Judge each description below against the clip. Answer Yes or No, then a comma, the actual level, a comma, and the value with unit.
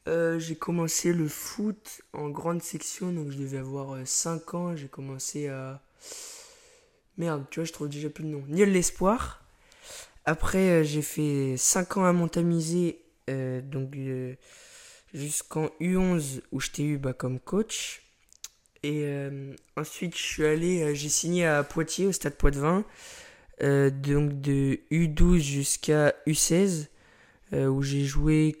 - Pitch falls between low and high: Yes, medium, 155 Hz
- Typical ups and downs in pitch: Yes, average, 3.8 semitones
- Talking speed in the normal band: Yes, average, 155 wpm